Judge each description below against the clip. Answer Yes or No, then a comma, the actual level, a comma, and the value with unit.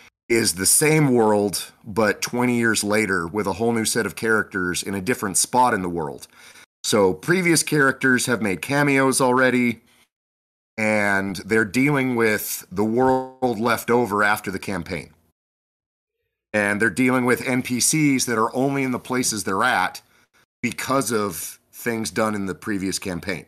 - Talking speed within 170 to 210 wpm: No, average, 155 wpm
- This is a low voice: Yes, low, 115 Hz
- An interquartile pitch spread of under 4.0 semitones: No, average, 4.3 semitones